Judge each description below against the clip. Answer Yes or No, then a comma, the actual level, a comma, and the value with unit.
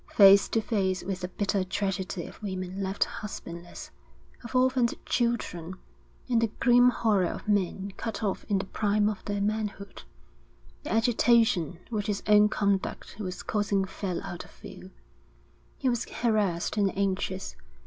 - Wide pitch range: No, narrow, 2.6 semitones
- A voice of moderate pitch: No, high, 200 Hz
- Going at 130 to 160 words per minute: Yes, average, 150 wpm